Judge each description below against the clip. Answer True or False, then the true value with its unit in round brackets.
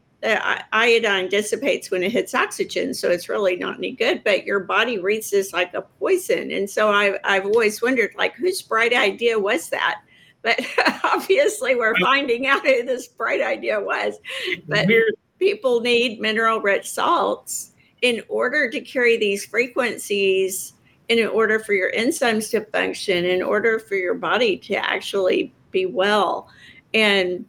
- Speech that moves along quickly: False (155 wpm)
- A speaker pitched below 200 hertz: False (225 Hz)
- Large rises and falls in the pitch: True (8.0 semitones)